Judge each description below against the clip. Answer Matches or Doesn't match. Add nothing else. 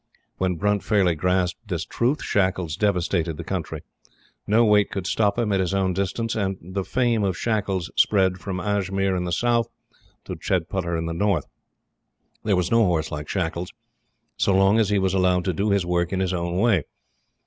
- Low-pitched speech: Matches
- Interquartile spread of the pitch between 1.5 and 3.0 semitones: Matches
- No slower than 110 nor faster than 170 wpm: Doesn't match